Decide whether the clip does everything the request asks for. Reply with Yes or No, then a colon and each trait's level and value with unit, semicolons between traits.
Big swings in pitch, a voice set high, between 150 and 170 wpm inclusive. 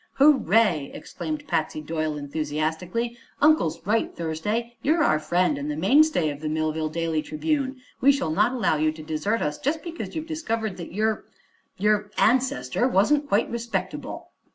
Yes: wide, 8.7 semitones; high, 205 Hz; average, 155 wpm